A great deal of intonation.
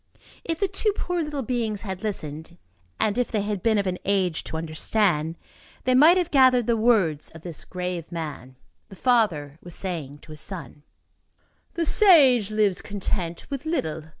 Yes: wide, 7.1 semitones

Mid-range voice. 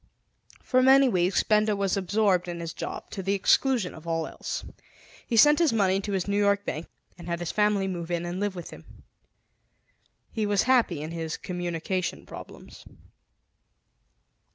No: high, 195 Hz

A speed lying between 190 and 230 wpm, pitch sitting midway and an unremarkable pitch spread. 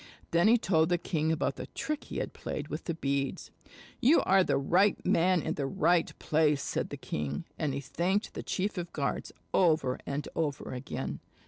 Yes: average, 200 wpm; medium, 160 Hz; average, 4.4 semitones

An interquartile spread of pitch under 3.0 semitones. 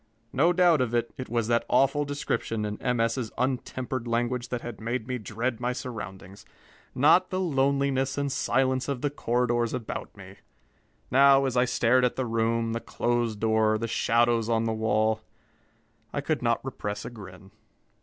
Yes: narrow, 2.6 semitones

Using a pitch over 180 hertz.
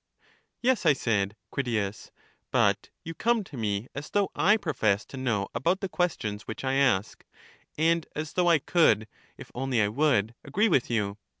No: low, 135 Hz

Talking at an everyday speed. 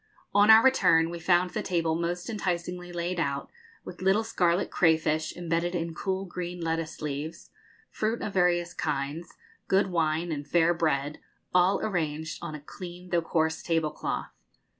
Yes: average, 155 wpm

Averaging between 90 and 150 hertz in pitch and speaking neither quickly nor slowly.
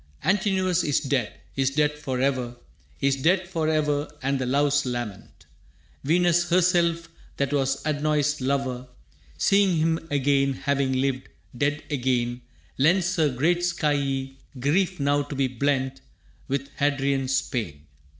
No: medium, 140 Hz; slow, 125 wpm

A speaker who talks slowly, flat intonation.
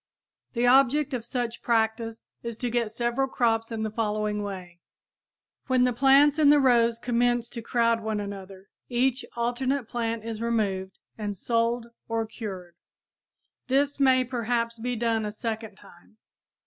No: average, 150 wpm; narrow, 2.1 semitones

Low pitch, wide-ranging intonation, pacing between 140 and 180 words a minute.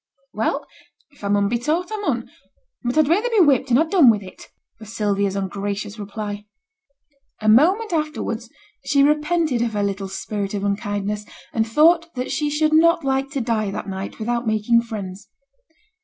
No: high, 235 Hz; wide, 6.8 semitones; average, 175 wpm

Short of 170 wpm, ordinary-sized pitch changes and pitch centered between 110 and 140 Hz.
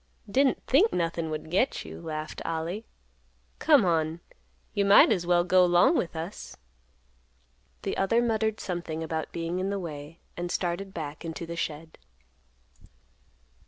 No: average, 145 wpm; average, 3.5 semitones; medium, 175 Hz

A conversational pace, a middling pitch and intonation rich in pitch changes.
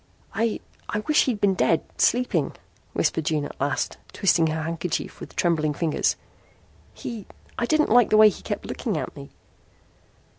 Yes: average, 160 wpm; medium, 180 Hz; wide, 6.1 semitones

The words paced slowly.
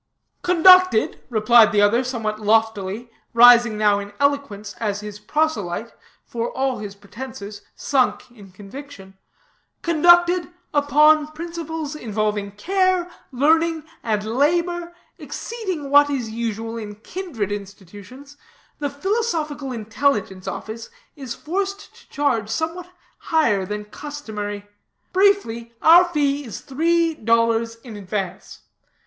Yes: slow, 115 wpm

